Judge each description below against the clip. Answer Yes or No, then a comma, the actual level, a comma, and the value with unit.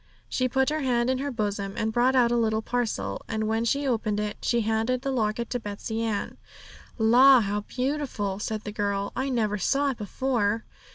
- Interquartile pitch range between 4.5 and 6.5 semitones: No, average, 3.3 semitones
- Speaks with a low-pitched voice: No, high, 225 Hz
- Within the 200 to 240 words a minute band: Yes, fast, 205 wpm